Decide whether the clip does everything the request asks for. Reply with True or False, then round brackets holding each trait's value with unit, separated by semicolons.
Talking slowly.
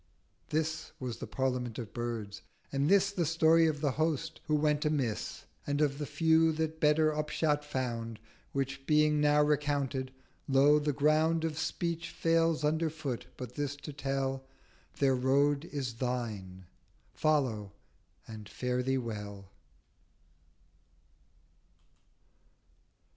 True (125 wpm)